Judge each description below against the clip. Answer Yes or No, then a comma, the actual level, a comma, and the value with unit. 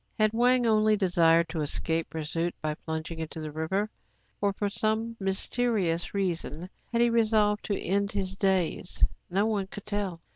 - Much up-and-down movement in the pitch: No, average, 4.4 semitones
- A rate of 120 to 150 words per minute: No, average, 160 wpm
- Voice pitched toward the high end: Yes, high, 195 Hz